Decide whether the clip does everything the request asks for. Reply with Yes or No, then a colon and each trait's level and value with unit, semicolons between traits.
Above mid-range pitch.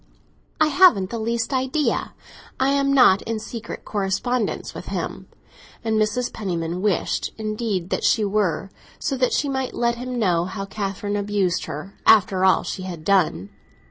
Yes: high, 215 Hz